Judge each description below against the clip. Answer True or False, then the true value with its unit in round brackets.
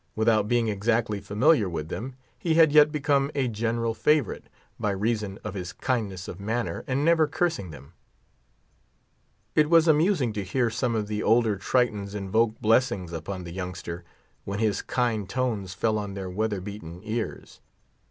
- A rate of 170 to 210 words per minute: False (160 wpm)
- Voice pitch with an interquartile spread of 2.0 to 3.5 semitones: False (4.3 semitones)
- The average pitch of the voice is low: True (110 Hz)